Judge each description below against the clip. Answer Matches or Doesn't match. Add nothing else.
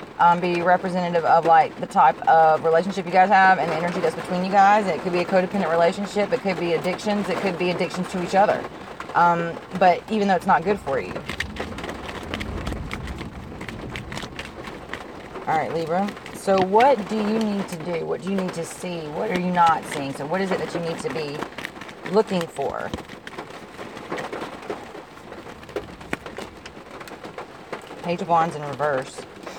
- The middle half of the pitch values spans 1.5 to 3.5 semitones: Matches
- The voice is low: Doesn't match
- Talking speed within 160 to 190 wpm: Matches